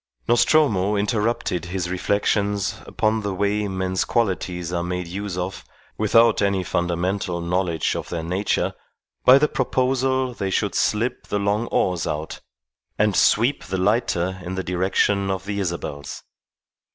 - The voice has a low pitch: Yes, very low, 95 Hz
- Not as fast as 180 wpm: Yes, average, 140 wpm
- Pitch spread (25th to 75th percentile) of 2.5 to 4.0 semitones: Yes, average, 2.9 semitones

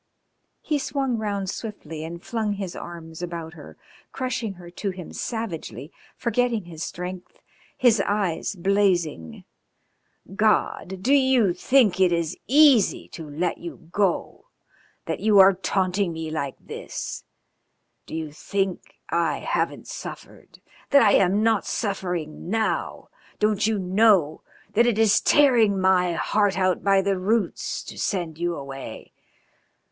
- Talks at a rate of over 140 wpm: No, slow, 135 wpm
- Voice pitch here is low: No, high, 190 Hz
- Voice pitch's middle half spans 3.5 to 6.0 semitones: Yes, average, 4.1 semitones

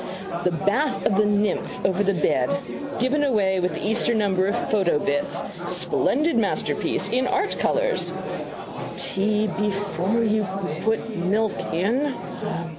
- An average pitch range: Yes, average, 3.5 semitones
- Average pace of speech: No, slow, 130 wpm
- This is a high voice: Yes, high, 210 Hz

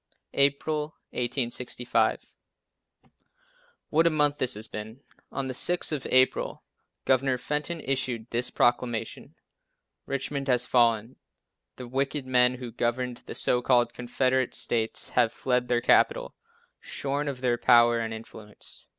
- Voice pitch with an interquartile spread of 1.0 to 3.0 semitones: Yes, narrow, 2.4 semitones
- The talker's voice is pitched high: No, low, 125 Hz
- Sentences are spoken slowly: Yes, slow, 130 wpm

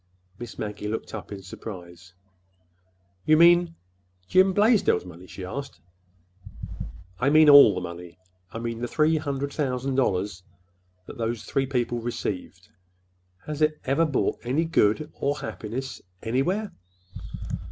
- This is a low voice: Yes, low, 120 Hz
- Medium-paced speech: No, slow, 120 wpm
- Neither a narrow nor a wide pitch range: No, wide, 8.0 semitones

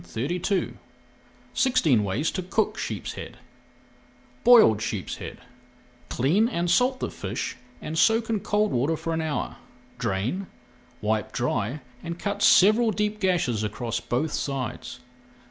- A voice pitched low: No, medium, 165 Hz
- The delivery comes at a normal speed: No, slow, 130 wpm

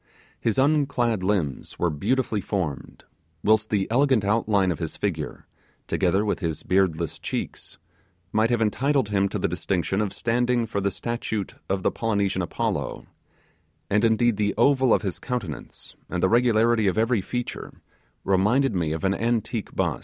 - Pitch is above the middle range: No, low, 105 Hz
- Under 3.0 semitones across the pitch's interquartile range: No, average, 3.7 semitones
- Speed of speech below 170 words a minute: Yes, average, 160 wpm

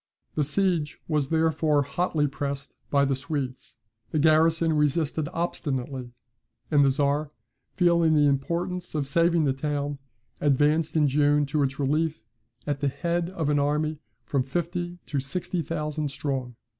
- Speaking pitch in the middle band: Yes, medium, 150 Hz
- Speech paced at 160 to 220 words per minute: No, average, 145 wpm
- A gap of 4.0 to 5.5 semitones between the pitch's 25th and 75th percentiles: No, narrow, 2.6 semitones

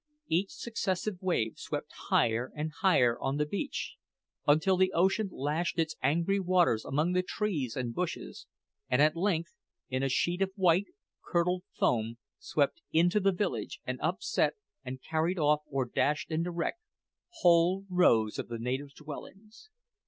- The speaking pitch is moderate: Yes, medium, 165 Hz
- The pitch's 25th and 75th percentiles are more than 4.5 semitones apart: Yes, average, 5.1 semitones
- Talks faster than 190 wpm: No, average, 150 wpm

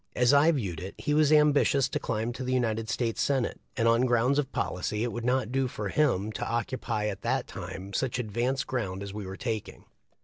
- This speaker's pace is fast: Yes, fast, 215 wpm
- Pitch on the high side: No, low, 120 Hz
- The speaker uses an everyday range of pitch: Yes, average, 3.7 semitones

